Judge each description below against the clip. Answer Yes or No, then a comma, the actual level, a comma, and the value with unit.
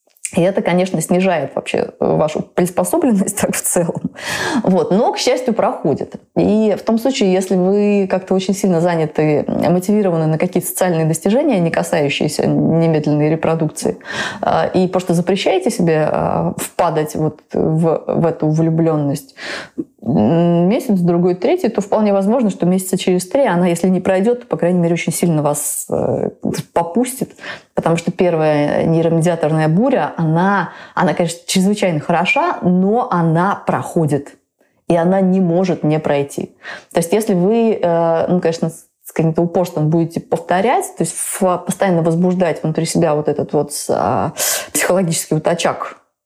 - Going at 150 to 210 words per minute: No, average, 140 wpm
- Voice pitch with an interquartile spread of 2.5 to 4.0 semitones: Yes, average, 2.9 semitones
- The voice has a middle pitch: Yes, medium, 175 Hz